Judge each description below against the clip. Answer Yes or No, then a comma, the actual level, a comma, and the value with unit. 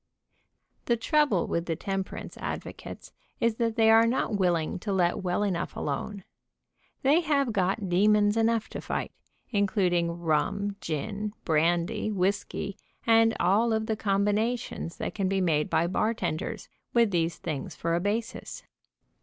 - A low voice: No, high, 200 Hz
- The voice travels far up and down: No, average, 4.3 semitones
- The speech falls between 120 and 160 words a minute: Yes, average, 145 wpm